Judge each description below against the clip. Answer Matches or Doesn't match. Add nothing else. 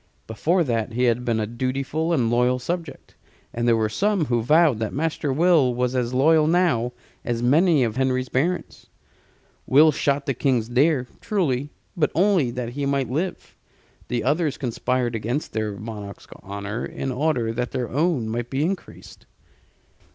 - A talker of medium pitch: Doesn't match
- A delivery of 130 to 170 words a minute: Matches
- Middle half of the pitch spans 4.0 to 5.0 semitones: Matches